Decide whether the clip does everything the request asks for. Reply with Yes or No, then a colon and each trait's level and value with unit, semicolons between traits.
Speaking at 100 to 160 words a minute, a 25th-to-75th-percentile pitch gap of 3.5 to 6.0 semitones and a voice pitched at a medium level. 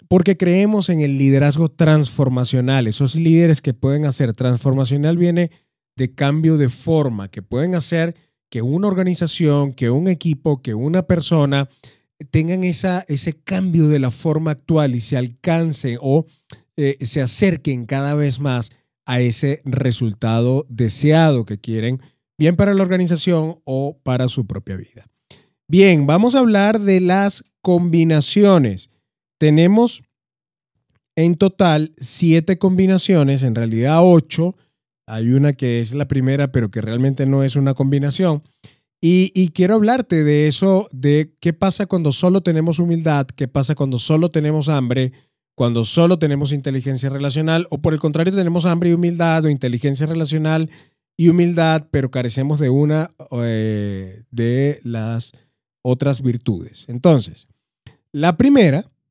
Yes: average, 140 wpm; average, 4.6 semitones; medium, 145 Hz